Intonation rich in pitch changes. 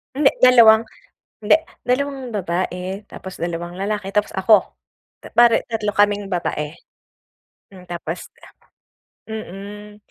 No: average, 3.4 semitones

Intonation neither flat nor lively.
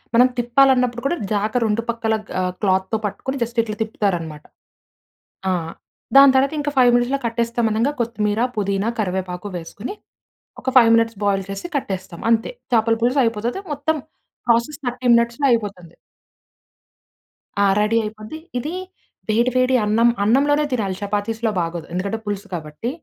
Yes: average, 3.4 semitones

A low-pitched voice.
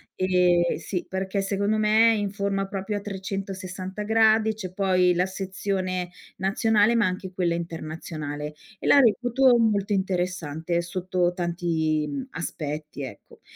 No: high, 190 Hz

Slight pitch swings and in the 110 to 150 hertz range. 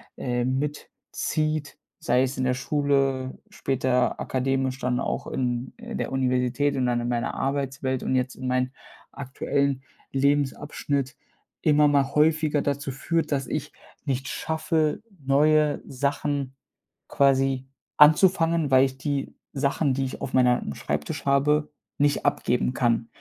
Yes: narrow, 2.1 semitones; low, 135 Hz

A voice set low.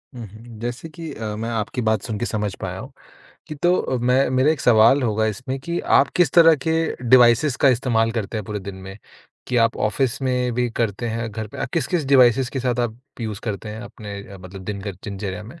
Yes: low, 115 Hz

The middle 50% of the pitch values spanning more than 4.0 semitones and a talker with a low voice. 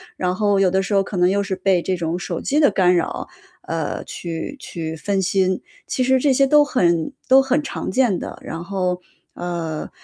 No: average, 4.4 semitones; high, 190 Hz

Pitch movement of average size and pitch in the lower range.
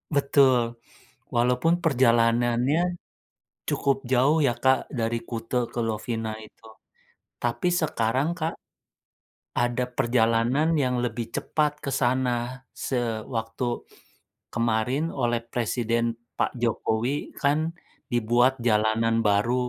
No: narrow, 2.3 semitones; low, 120 Hz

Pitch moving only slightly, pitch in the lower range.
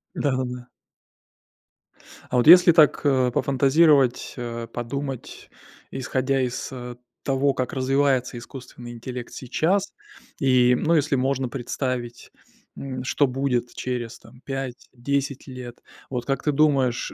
Yes: narrow, 2.0 semitones; low, 130 Hz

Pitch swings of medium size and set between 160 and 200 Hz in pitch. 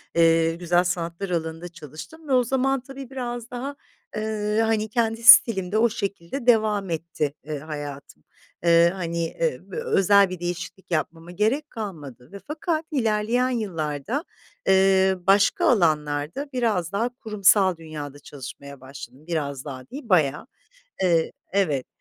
No: wide, 6.0 semitones; high, 190 Hz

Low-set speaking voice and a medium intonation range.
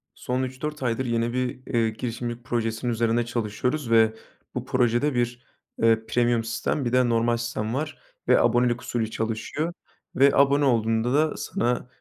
No: low, 120 Hz; narrow, 2.0 semitones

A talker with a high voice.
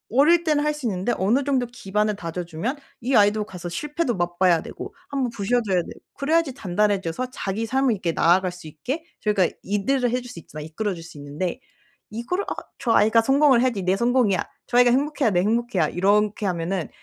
Yes: high, 210 Hz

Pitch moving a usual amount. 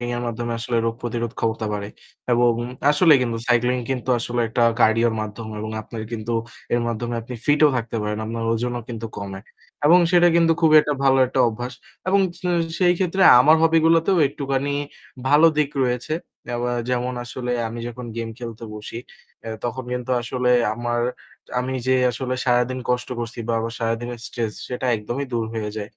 No: narrow, 2.3 semitones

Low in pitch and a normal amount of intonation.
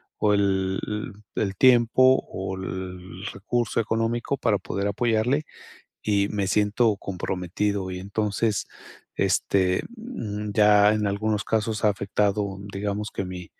No: low, 105 Hz; narrow, 2.1 semitones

